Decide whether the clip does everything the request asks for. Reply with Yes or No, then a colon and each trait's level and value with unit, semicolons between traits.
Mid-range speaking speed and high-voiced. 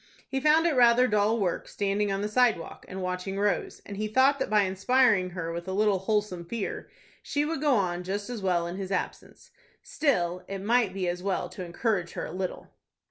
No: fast, 210 wpm; high, 200 Hz